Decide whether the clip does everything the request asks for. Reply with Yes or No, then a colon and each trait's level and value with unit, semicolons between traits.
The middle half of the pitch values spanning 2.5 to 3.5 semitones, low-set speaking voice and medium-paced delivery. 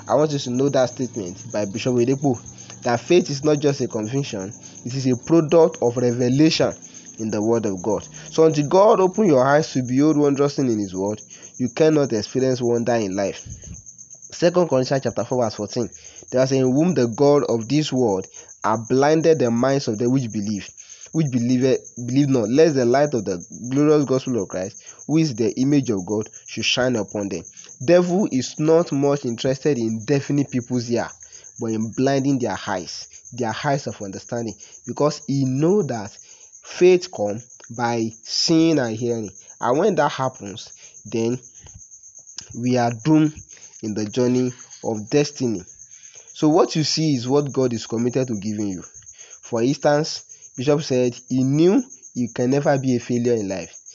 No: average, 4.1 semitones; low, 125 Hz; average, 180 wpm